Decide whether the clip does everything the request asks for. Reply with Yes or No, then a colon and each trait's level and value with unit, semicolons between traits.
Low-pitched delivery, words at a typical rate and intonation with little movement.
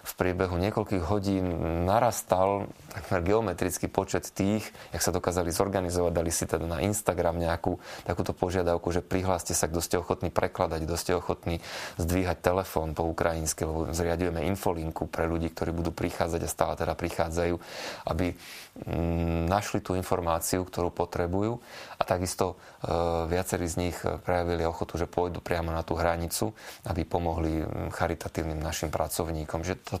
Yes: very low, 90 Hz; average, 145 wpm; narrow, 2.3 semitones